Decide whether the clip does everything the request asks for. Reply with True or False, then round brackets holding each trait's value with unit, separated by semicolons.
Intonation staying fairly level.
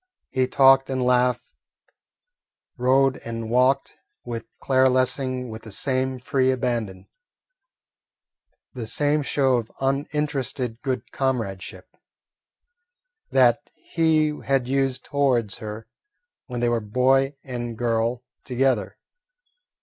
True (2.2 semitones)